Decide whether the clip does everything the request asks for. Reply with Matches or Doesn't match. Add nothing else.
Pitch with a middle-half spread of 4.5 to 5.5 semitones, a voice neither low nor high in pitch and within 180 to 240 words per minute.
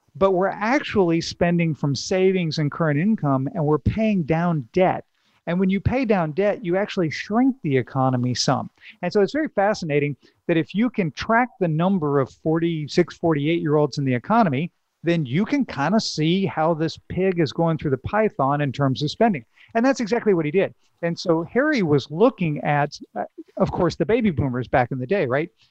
Matches